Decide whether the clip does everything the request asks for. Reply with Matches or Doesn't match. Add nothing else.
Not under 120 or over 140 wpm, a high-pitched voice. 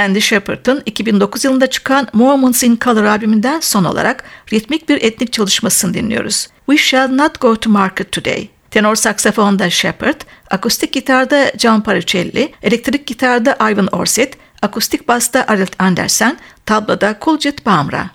Matches